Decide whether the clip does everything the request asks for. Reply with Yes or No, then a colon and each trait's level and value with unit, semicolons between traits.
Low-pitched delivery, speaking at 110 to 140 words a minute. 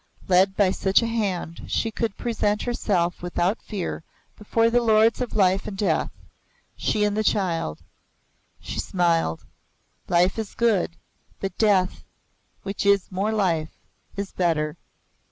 No: high, 195 Hz; slow, 135 wpm